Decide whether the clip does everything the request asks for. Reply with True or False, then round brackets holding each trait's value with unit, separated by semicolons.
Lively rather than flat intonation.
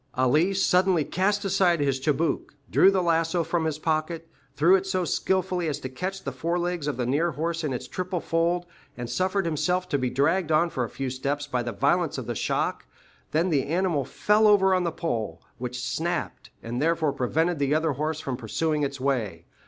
False (4.4 semitones)